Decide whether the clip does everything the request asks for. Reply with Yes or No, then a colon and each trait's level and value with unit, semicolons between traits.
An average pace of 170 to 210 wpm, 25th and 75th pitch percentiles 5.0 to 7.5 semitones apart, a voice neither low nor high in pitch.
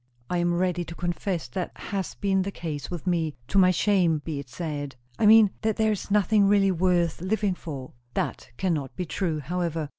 No: average, 200 wpm; average, 3.3 semitones; medium, 180 Hz